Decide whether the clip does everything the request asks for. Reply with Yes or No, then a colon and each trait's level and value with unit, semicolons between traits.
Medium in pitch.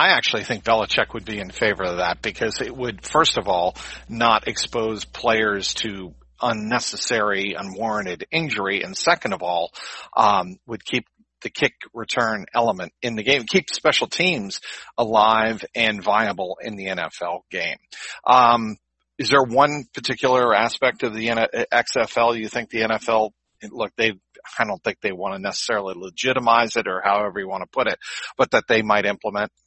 No: low, 115 Hz